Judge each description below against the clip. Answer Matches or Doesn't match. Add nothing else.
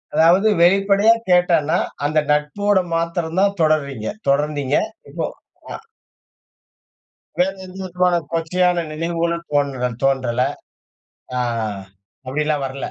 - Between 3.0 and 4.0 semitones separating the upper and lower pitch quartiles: Matches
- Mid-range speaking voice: Matches